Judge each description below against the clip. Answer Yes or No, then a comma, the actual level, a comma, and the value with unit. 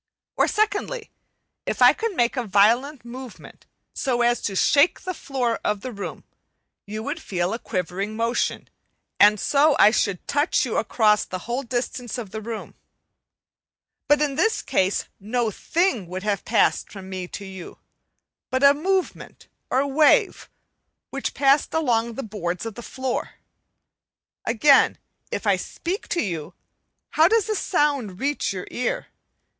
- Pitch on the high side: Yes, high, 240 Hz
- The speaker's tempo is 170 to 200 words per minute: No, average, 155 wpm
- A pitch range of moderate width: No, wide, 5.7 semitones